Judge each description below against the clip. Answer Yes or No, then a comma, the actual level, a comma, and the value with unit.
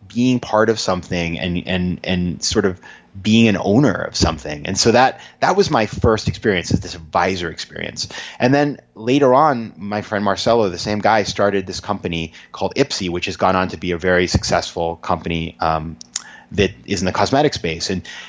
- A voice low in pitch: Yes, very low, 95 Hz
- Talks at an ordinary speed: Yes, average, 195 wpm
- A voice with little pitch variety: No, average, 3.1 semitones